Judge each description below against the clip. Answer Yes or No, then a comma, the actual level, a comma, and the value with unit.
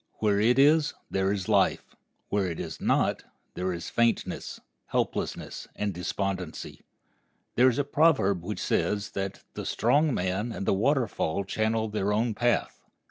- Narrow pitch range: No, average, 4.0 semitones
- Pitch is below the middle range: Yes, low, 105 Hz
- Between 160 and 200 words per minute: No, average, 150 wpm